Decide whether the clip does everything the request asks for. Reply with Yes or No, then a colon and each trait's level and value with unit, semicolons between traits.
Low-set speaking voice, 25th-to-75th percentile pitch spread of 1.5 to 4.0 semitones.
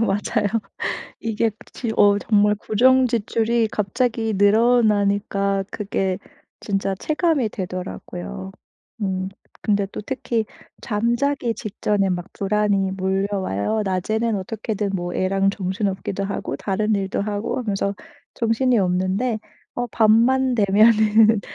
No: high, 210 Hz; narrow, 2.6 semitones